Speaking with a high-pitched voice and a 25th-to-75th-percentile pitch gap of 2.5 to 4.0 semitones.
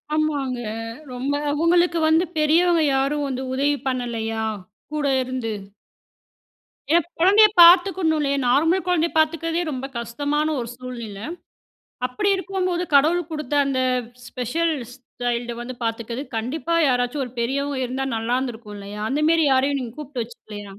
No: very high, 280 Hz; average, 4.8 semitones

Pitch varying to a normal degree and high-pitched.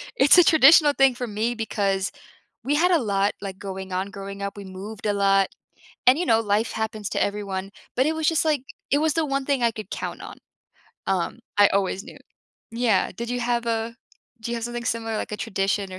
Yes: average, 4.0 semitones; high, 225 Hz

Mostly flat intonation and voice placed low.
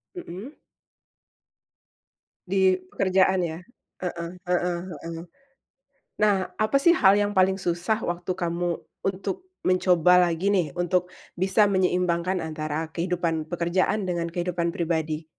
No: narrow, 2.0 semitones; medium, 180 Hz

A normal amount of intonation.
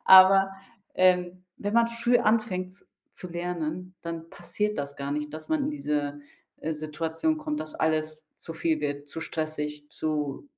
Yes: average, 4.0 semitones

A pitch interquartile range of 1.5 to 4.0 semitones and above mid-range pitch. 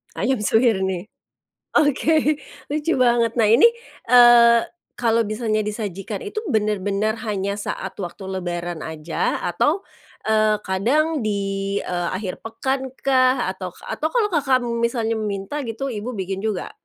No: average, 4.4 semitones; high, 220 Hz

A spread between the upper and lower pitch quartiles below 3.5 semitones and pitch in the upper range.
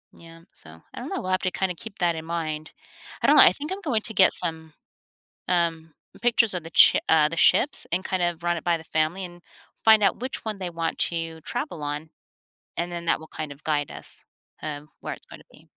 No: average, 2.8 semitones; medium, 170 Hz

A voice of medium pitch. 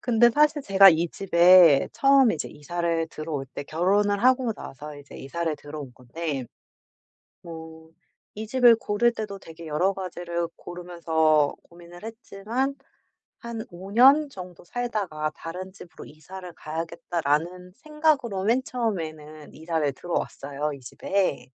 Yes: medium, 175 Hz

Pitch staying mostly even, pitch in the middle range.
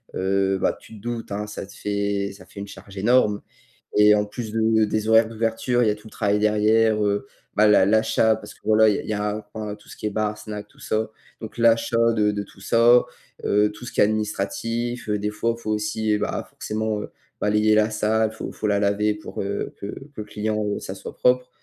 No: narrow, 1.2 semitones; low, 105 Hz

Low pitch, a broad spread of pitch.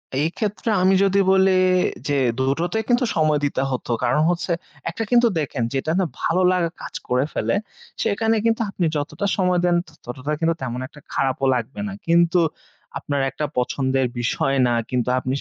No: medium, 155 Hz; wide, 6.1 semitones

